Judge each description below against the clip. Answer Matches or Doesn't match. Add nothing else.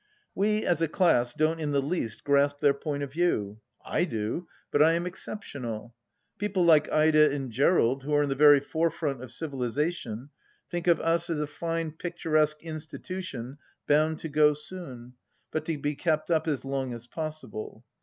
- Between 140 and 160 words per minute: Doesn't match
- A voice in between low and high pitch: Matches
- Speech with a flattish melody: Doesn't match